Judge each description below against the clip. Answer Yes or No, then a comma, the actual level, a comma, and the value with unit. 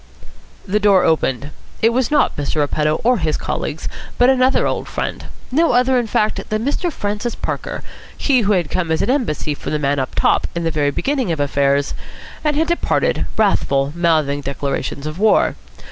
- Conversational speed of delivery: Yes, average, 185 wpm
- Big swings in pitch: Yes, wide, 9.0 semitones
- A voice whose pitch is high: No, medium, 180 Hz